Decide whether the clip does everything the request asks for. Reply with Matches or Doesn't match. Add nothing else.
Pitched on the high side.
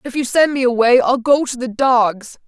Matches